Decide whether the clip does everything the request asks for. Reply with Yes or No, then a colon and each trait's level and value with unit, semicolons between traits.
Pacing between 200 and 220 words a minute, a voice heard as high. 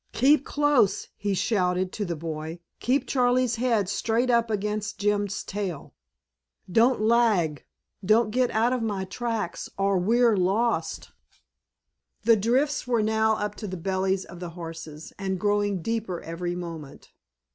No: average, 145 wpm; high, 205 Hz